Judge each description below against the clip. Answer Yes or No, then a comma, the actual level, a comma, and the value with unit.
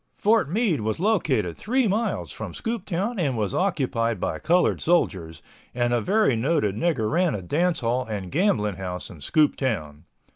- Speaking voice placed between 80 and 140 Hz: Yes, low, 135 Hz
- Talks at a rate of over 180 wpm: No, average, 160 wpm